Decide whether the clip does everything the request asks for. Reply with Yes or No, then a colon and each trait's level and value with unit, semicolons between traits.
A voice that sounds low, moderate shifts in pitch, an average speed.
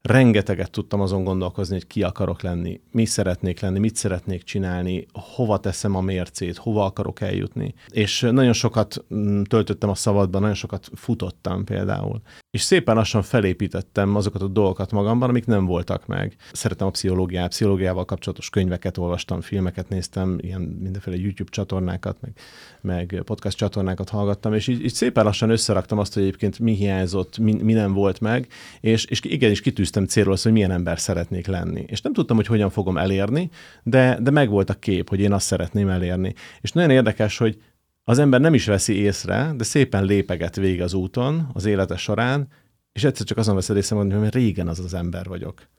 No: low, 100 Hz; average, 3.0 semitones; fast, 180 wpm